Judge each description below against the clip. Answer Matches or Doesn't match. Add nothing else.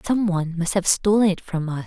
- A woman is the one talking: Matches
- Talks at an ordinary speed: Doesn't match